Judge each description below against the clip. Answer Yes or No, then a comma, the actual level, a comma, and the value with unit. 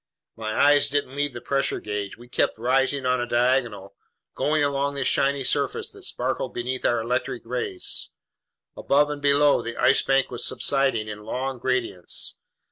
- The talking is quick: No, average, 165 wpm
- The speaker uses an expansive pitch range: No, average, 3.0 semitones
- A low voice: Yes, low, 130 Hz